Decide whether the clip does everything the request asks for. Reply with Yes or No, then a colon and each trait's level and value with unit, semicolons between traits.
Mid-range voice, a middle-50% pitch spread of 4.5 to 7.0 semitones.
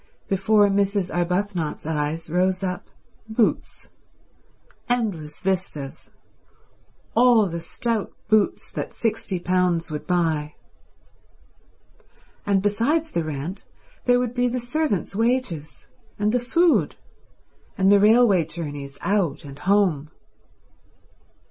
No: high, 195 Hz; average, 5.1 semitones